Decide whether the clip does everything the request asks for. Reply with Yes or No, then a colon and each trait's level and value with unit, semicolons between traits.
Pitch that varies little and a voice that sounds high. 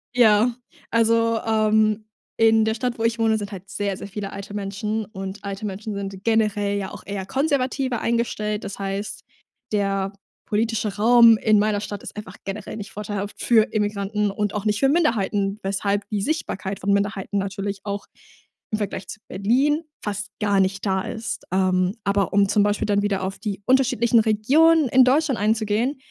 Yes: narrow, 2.2 semitones; high, 210 Hz